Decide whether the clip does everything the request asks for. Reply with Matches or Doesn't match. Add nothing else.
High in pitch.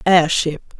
Doesn't match